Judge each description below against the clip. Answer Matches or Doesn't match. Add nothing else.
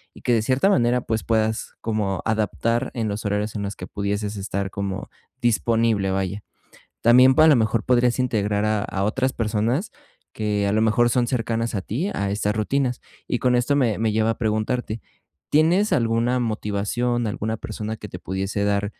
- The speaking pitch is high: Doesn't match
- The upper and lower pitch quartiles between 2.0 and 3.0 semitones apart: Matches